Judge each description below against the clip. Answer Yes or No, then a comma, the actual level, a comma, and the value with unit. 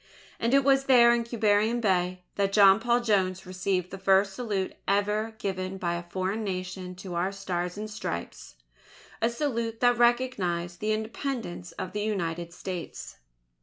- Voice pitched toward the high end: Yes, high, 195 Hz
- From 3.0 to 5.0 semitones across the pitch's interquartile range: Yes, average, 3.8 semitones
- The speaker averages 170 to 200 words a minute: No, average, 160 wpm